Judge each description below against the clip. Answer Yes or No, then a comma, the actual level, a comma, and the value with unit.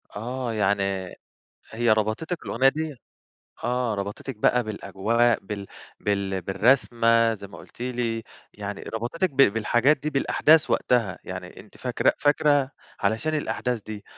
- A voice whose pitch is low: Yes, low, 115 Hz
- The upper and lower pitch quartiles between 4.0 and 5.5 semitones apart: Yes, average, 4.3 semitones